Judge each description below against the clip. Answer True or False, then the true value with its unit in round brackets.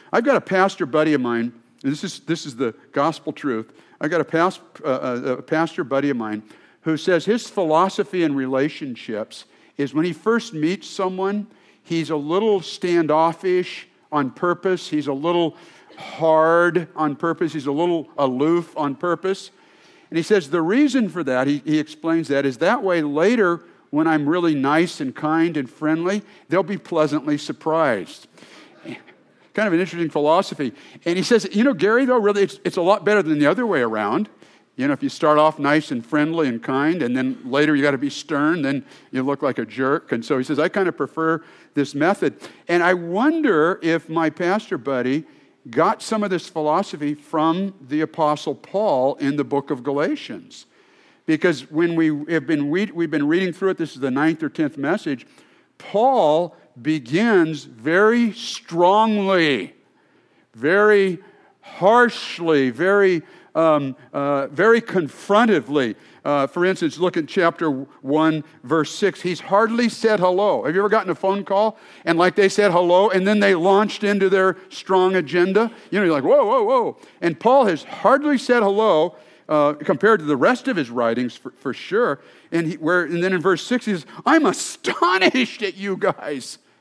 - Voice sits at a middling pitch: True (170 Hz)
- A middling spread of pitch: True (4.6 semitones)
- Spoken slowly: False (180 wpm)